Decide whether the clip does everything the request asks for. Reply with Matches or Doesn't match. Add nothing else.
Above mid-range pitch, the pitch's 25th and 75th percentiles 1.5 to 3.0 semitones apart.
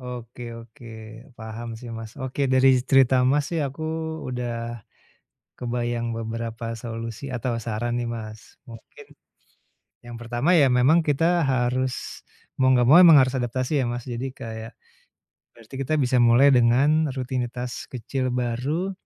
Doesn't match